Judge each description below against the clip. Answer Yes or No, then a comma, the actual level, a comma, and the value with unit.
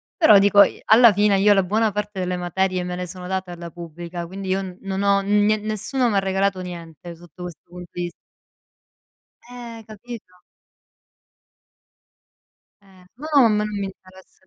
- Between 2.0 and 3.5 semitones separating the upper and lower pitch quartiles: Yes, narrow, 2.6 semitones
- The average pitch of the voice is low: No, high, 190 Hz